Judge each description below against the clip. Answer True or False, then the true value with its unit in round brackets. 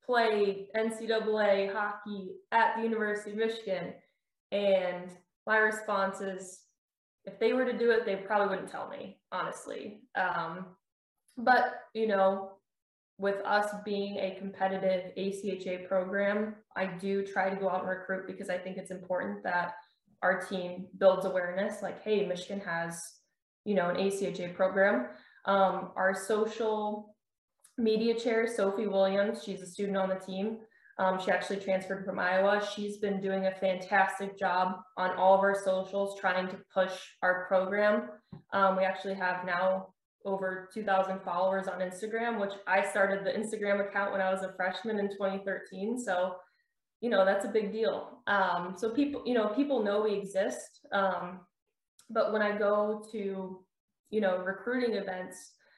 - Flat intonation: True (1.9 semitones)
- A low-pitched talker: False (195 Hz)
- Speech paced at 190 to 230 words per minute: False (155 wpm)